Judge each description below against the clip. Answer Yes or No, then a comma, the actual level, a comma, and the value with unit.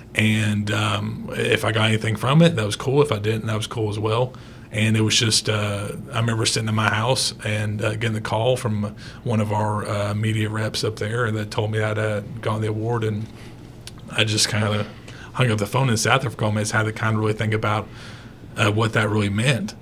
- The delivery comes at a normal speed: No, fast, 245 wpm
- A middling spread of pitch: No, narrow, 1.4 semitones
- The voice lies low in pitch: Yes, low, 110 Hz